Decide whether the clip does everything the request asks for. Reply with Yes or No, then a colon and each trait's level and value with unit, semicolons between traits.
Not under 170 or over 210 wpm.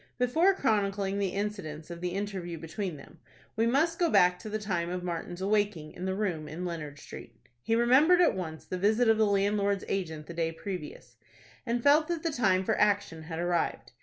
Yes: average, 200 wpm